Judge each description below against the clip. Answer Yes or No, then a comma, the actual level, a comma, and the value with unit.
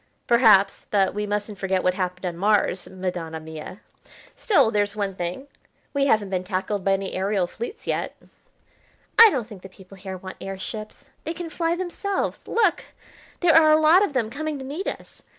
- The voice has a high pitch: Yes, high, 205 Hz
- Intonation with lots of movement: Yes, wide, 7.7 semitones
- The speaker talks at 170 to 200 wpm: Yes, average, 185 wpm